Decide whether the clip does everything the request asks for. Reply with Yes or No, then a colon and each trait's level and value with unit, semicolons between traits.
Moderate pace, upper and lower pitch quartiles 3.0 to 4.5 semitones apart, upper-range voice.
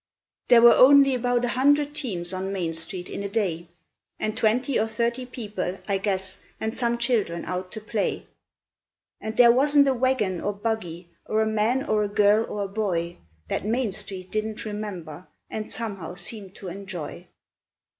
Yes: average, 175 wpm; average, 4.0 semitones; high, 215 Hz